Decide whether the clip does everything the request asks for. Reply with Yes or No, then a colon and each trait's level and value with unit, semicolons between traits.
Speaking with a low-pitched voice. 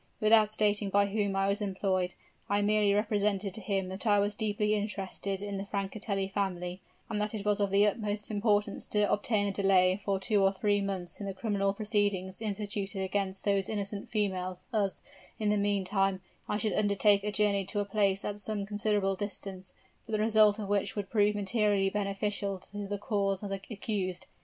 No: high, 200 Hz